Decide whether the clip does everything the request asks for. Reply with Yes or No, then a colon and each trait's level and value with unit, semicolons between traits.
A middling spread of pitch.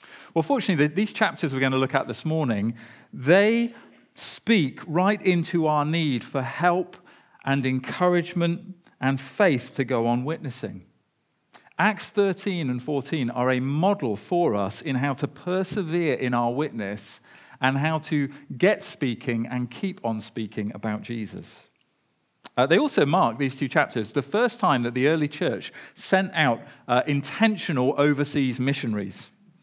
No: wide, 6.1 semitones